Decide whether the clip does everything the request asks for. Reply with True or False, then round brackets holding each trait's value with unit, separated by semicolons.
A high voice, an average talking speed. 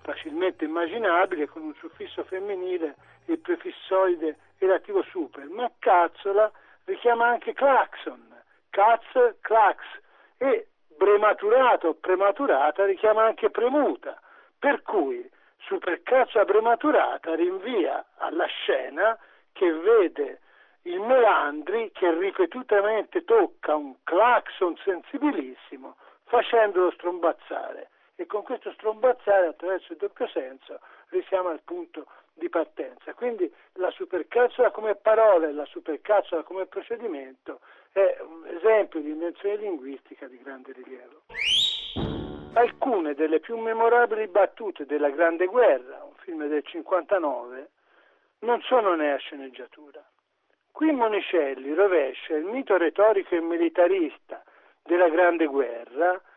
False (220 Hz; 110 wpm)